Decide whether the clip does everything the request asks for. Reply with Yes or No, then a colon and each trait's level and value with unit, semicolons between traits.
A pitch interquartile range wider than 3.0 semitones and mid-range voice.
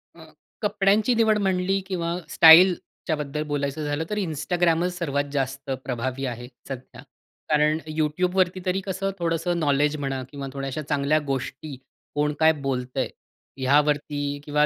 Yes: average, 4.2 semitones; medium, 150 Hz